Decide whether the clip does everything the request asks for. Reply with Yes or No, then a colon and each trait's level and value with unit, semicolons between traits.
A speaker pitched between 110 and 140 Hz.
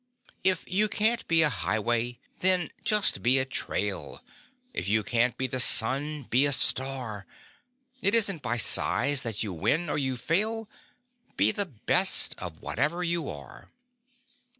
Yes: low, 135 Hz